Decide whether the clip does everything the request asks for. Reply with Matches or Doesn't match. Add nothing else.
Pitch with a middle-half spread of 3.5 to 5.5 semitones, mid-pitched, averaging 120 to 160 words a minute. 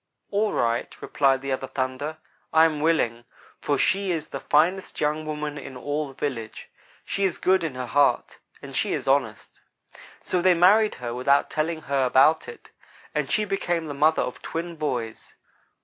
Doesn't match